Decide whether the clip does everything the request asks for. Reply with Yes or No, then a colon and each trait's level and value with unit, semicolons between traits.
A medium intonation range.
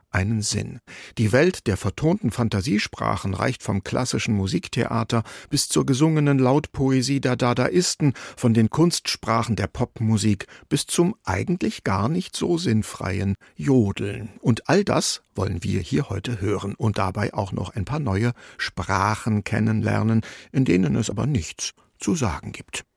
Yes: average, 4.0 semitones